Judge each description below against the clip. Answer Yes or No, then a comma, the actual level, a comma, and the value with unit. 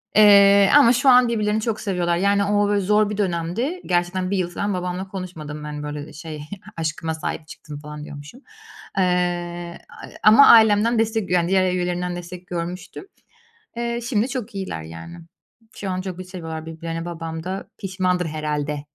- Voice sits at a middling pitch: Yes, medium, 180 Hz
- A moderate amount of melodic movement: Yes, average, 3.8 semitones